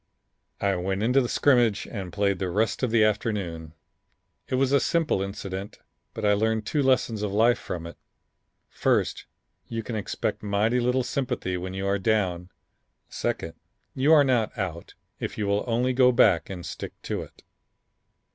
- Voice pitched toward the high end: No, low, 105 Hz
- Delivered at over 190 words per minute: No, average, 170 wpm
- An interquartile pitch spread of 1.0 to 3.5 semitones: No, average, 4.1 semitones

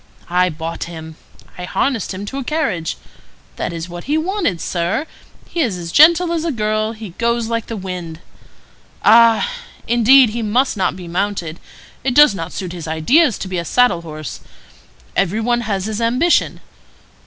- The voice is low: No, high, 215 Hz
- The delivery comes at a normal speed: Yes, average, 175 wpm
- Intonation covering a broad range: Yes, wide, 6.0 semitones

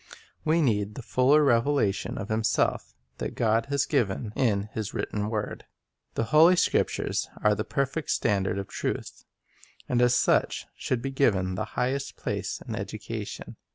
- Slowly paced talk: No, average, 155 wpm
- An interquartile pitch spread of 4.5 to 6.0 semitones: Yes, average, 4.8 semitones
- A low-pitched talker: Yes, low, 115 Hz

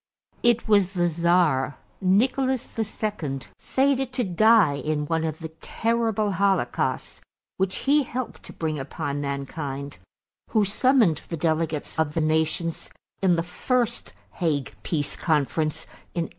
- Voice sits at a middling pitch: Yes, medium, 170 Hz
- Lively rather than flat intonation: Yes, wide, 6.1 semitones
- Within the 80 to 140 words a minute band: Yes, slow, 135 wpm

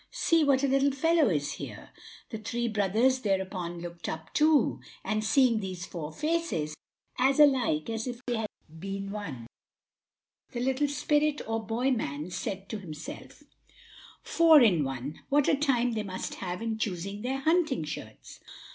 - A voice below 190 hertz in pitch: No, high, 225 Hz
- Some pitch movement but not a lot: No, wide, 6.6 semitones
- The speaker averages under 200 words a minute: Yes, average, 160 wpm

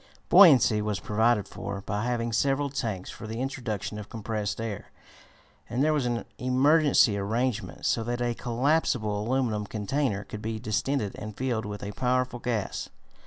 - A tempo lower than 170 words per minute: Yes, average, 160 wpm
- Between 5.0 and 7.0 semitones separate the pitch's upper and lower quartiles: No, average, 3.4 semitones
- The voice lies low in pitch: Yes, low, 115 Hz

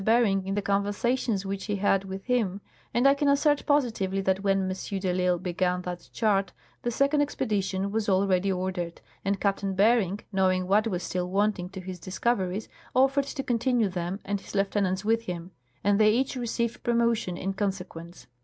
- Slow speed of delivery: No, average, 180 wpm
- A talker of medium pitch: No, high, 195 Hz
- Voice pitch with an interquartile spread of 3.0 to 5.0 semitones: Yes, average, 3.4 semitones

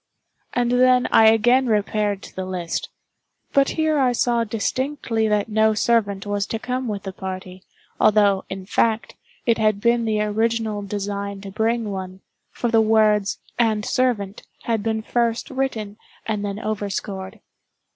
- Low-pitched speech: No, high, 215 Hz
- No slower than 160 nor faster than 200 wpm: No, average, 145 wpm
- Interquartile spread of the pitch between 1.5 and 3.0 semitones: Yes, narrow, 2.5 semitones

